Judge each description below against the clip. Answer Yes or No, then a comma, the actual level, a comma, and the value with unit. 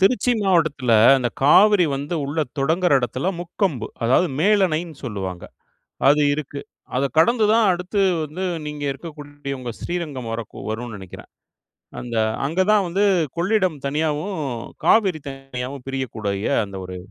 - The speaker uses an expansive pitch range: Yes, wide, 5.9 semitones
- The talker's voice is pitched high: No, medium, 150 Hz